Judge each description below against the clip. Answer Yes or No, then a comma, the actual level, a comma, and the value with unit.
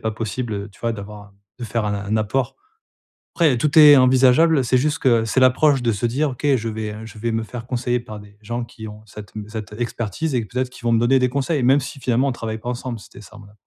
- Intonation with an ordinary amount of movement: Yes, average, 3.1 semitones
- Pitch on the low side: Yes, low, 120 Hz